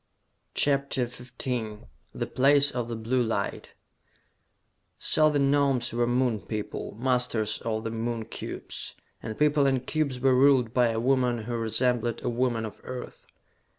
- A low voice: Yes, low, 125 Hz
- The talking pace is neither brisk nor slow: Yes, average, 150 wpm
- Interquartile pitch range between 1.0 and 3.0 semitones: Yes, average, 2.7 semitones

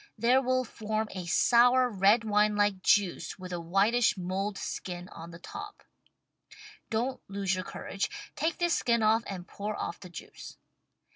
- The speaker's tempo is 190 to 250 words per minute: No, average, 160 wpm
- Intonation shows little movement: No, average, 4.1 semitones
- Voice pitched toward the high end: Yes, high, 210 Hz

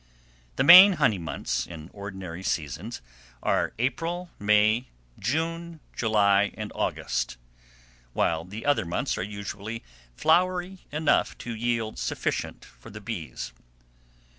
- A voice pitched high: No, low, 110 Hz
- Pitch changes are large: Yes, wide, 8.0 semitones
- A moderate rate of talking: No, slow, 115 wpm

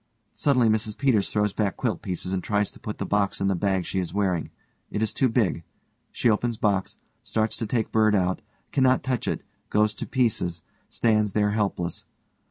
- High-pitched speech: No, low, 105 Hz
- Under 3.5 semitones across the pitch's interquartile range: Yes, narrow, 2.6 semitones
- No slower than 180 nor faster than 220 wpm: Yes, average, 190 wpm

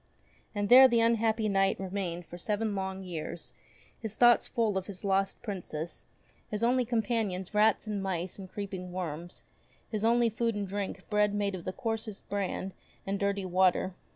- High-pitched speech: Yes, high, 200 Hz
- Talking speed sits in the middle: Yes, average, 170 wpm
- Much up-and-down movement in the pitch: No, average, 2.8 semitones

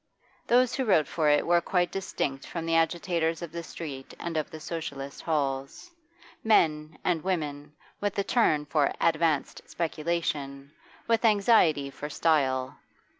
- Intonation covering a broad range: No, average, 3.1 semitones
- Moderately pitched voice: Yes, medium, 160 Hz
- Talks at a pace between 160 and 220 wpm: No, average, 145 wpm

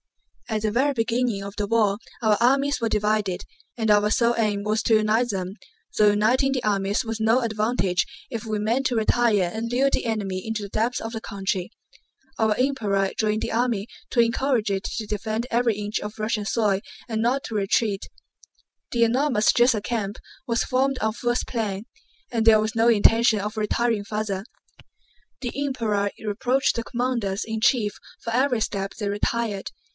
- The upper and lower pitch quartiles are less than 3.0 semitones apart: Yes, narrow, 2.4 semitones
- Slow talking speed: No, average, 180 wpm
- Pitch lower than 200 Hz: No, high, 220 Hz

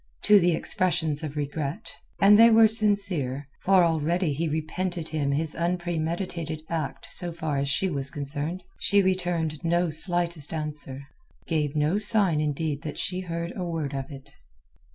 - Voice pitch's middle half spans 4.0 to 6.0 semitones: No, average, 3.3 semitones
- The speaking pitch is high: No, medium, 165 Hz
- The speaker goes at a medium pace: Yes, average, 150 wpm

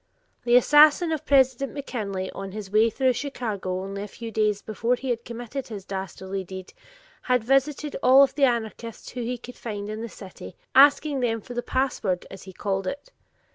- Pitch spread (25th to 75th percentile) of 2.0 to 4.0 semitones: No, average, 4.9 semitones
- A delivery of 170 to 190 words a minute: Yes, average, 180 wpm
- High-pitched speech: Yes, high, 230 Hz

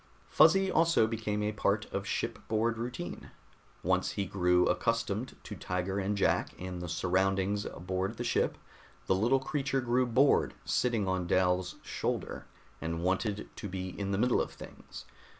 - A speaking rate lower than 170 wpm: Yes, average, 155 wpm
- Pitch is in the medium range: No, low, 100 Hz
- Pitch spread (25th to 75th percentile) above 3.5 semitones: Yes, average, 3.9 semitones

